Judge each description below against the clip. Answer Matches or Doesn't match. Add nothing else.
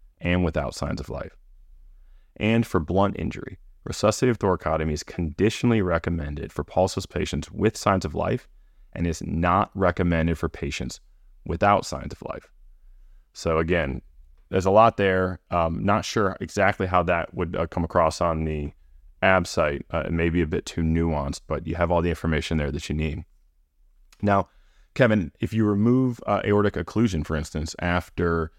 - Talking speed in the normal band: Matches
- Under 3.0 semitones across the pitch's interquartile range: Doesn't match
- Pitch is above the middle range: Doesn't match